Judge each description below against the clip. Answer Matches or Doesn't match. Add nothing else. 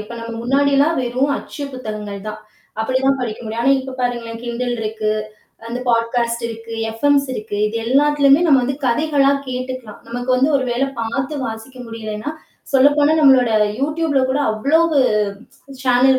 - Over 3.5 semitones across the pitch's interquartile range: Doesn't match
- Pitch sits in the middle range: Doesn't match